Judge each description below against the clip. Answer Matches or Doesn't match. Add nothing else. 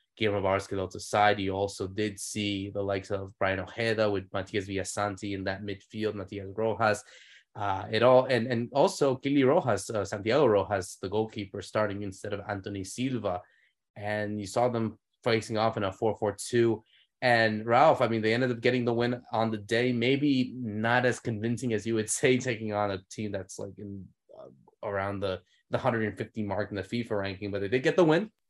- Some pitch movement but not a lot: Matches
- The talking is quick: Doesn't match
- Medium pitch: Doesn't match